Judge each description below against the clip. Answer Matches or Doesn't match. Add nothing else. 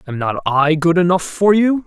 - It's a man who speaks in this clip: Matches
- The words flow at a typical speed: Doesn't match